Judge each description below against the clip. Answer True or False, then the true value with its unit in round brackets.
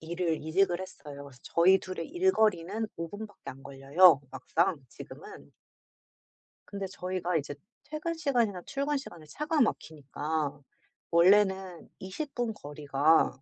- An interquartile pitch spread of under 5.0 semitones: False (5.3 semitones)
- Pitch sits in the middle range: True (180 Hz)